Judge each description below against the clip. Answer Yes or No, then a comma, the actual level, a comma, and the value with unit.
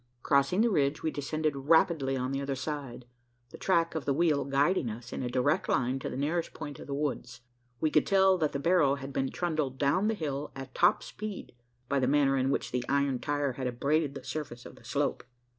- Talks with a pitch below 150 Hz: Yes, medium, 140 Hz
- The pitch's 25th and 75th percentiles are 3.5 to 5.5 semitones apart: No, average, 2.7 semitones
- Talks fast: Yes, fast, 225 wpm